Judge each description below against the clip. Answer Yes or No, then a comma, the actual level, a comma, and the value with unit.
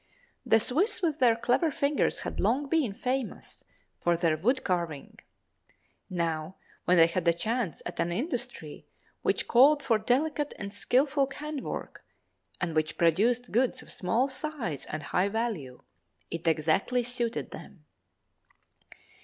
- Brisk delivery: No, average, 140 wpm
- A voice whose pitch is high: Yes, high, 230 Hz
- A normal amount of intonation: No, wide, 7.5 semitones